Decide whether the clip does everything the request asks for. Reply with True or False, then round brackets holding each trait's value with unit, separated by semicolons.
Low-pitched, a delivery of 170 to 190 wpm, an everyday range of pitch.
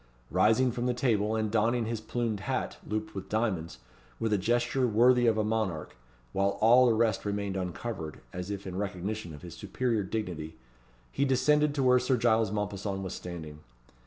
True (110 Hz; 180 wpm; 3.7 semitones)